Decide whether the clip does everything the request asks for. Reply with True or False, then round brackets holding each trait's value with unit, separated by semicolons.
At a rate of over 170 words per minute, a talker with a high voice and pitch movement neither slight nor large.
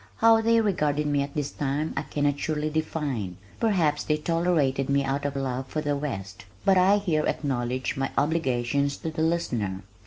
False (180 wpm; 145 Hz; 3.1 semitones)